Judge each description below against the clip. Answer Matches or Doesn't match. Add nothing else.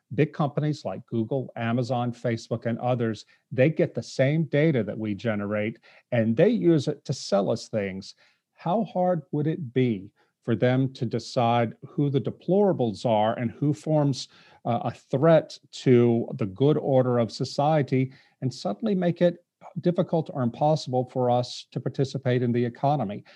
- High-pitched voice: Doesn't match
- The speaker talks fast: Doesn't match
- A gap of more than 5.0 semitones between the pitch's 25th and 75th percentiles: Doesn't match